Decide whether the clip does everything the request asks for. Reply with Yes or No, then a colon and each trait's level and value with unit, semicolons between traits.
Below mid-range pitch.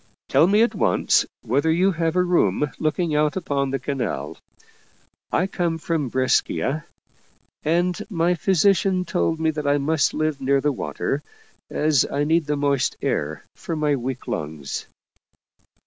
No: medium, 155 Hz